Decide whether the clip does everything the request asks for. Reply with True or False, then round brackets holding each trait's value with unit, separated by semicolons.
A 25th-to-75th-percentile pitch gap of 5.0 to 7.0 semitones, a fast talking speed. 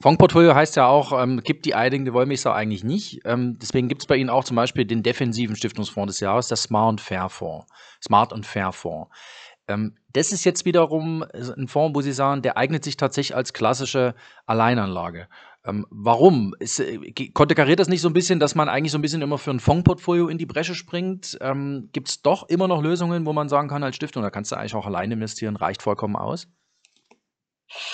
True (5.4 semitones; 215 wpm)